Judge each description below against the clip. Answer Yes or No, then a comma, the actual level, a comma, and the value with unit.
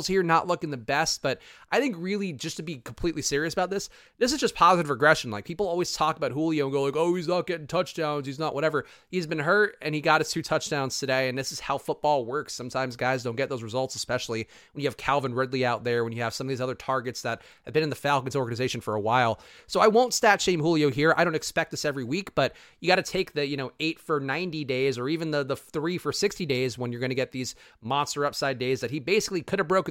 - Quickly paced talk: Yes, fast, 265 wpm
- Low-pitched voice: No, medium, 150 Hz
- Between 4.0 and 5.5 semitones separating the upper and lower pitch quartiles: Yes, average, 4.6 semitones